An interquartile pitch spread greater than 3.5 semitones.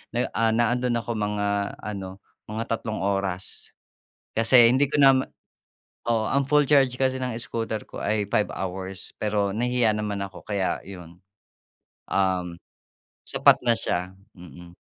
Yes: average, 3.9 semitones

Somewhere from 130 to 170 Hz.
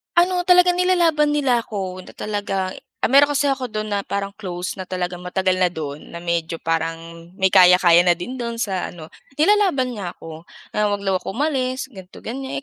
No: high, 200 Hz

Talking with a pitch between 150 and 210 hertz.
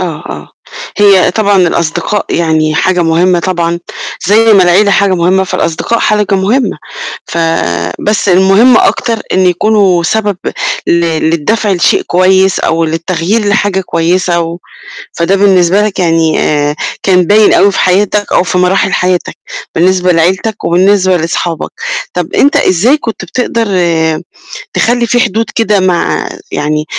Yes: medium, 185 Hz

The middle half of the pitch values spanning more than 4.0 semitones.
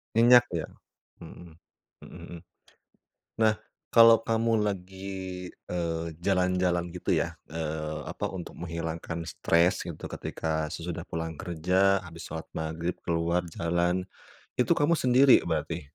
No: average, 2.8 semitones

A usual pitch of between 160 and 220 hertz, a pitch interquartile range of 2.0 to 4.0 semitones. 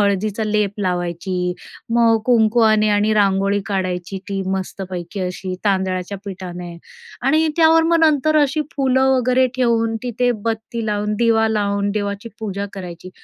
Yes: high, 210 Hz; average, 3.5 semitones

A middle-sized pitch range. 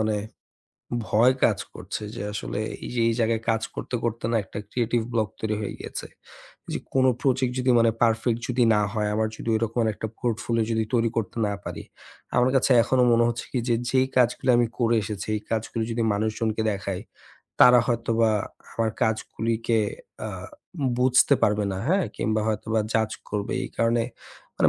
No: narrow, 1.7 semitones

